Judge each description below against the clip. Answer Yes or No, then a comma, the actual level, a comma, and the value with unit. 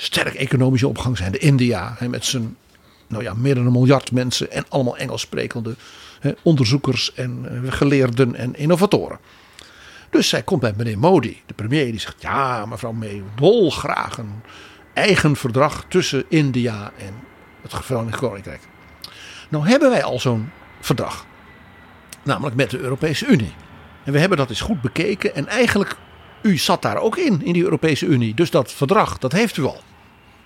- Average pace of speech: Yes, average, 165 wpm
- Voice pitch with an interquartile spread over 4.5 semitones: Yes, average, 5.2 semitones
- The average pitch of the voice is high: No, low, 125 Hz